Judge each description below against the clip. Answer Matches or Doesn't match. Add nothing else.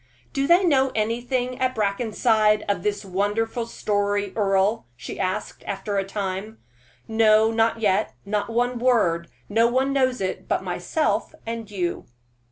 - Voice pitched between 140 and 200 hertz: Doesn't match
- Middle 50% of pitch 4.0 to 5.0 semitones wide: Doesn't match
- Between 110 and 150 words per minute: Matches